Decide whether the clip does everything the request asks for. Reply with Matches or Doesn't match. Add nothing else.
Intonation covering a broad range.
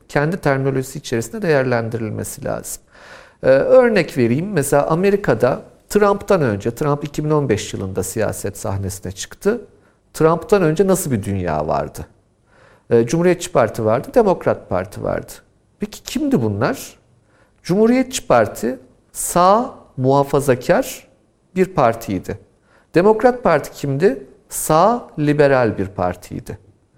Matches